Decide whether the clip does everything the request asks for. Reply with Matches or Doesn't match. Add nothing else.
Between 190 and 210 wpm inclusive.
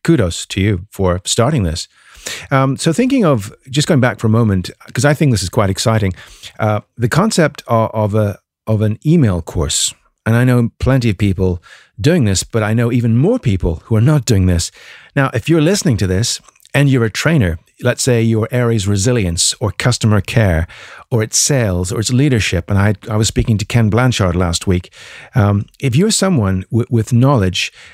Matches